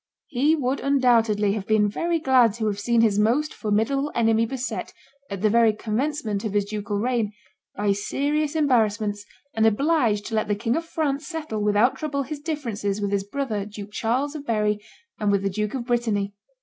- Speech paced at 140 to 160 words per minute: No, average, 190 wpm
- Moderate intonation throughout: Yes, average, 4.9 semitones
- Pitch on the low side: No, high, 225 Hz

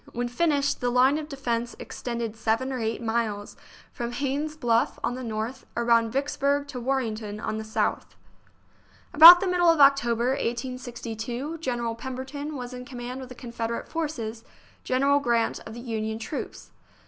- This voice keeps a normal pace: Yes, average, 160 wpm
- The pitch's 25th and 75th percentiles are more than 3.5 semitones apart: No, average, 3.2 semitones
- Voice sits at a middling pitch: No, high, 245 Hz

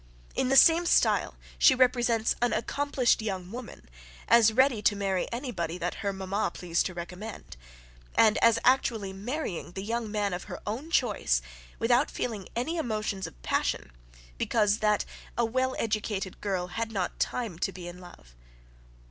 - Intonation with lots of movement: No, average, 4.2 semitones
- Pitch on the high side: Yes, high, 215 Hz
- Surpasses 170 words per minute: No, average, 165 wpm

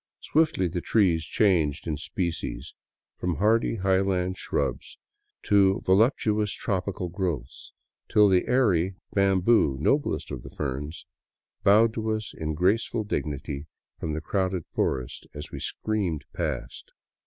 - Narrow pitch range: No, average, 4.8 semitones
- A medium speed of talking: No, slow, 125 wpm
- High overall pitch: No, very low, 95 Hz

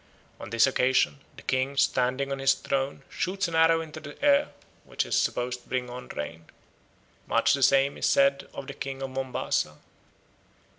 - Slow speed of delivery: No, average, 180 wpm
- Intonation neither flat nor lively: No, narrow, 1.8 semitones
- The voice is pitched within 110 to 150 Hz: Yes, low, 135 Hz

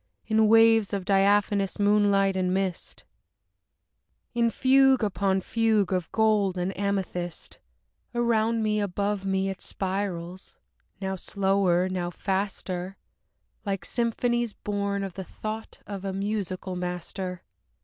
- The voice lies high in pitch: Yes, high, 195 Hz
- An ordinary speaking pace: No, slow, 120 wpm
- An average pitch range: No, narrow, 2.2 semitones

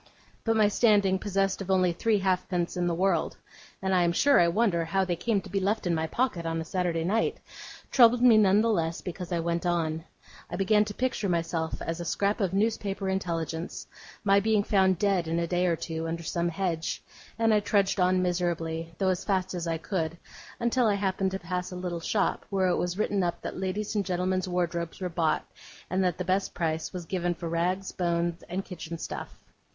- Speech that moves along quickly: Yes, fast, 215 wpm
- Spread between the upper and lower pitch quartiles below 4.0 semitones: Yes, narrow, 2.6 semitones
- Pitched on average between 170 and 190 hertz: Yes, medium, 185 Hz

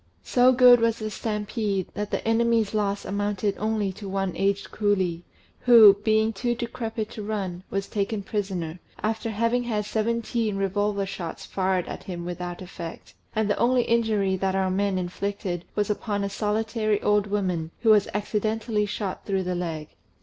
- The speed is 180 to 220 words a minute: No, average, 165 wpm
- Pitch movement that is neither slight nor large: No, narrow, 2.3 semitones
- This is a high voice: Yes, high, 205 Hz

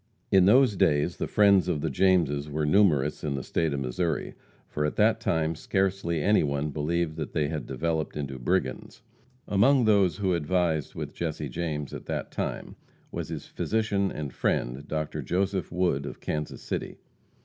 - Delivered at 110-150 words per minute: No, average, 170 wpm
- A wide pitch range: No, average, 4.3 semitones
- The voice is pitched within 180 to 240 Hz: No, very low, 80 Hz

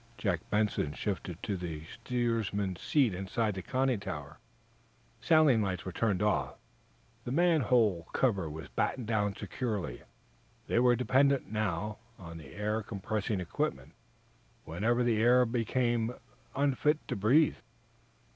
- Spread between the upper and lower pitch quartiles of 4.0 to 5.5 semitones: Yes, average, 4.7 semitones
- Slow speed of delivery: Yes, slow, 130 wpm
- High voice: No, low, 110 Hz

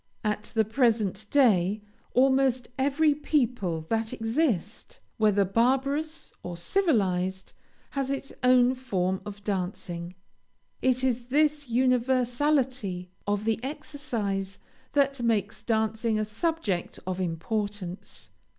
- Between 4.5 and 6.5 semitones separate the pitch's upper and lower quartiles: Yes, average, 5.1 semitones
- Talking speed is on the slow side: Yes, slow, 105 wpm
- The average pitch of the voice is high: Yes, high, 225 Hz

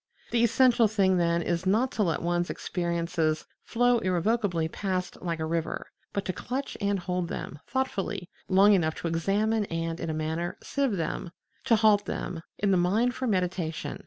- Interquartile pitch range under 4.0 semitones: No, average, 4.3 semitones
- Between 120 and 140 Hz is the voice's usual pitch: No, medium, 185 Hz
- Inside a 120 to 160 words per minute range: No, average, 175 wpm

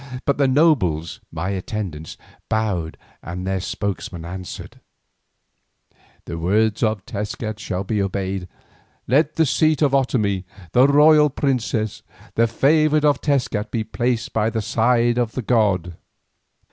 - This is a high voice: No, low, 110 Hz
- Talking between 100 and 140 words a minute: Yes, slow, 135 wpm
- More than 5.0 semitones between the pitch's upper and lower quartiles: Yes, wide, 5.6 semitones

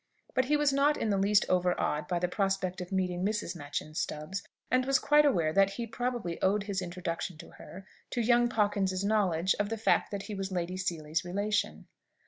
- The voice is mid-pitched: No, high, 195 Hz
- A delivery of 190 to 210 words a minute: Yes, average, 200 wpm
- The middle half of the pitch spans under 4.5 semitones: Yes, average, 3.6 semitones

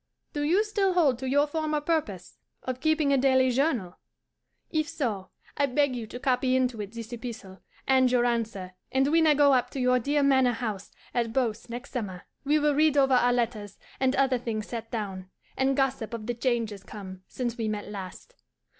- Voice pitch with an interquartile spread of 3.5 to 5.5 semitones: Yes, average, 3.9 semitones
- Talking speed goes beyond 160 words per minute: Yes, average, 200 wpm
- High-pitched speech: Yes, very high, 250 Hz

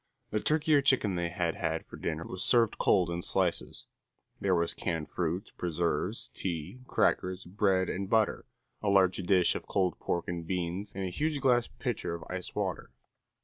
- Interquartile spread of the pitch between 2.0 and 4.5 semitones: Yes, average, 3.1 semitones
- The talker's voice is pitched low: Yes, very low, 95 Hz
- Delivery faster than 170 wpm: Yes, average, 180 wpm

